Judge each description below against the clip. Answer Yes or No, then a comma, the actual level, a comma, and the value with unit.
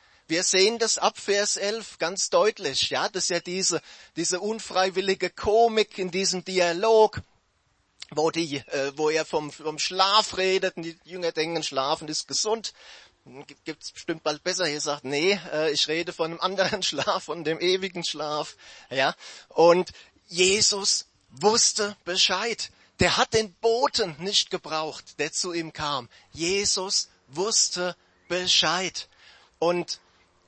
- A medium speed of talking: Yes, average, 145 wpm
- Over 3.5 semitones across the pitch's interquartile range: Yes, average, 3.9 semitones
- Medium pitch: Yes, medium, 180 Hz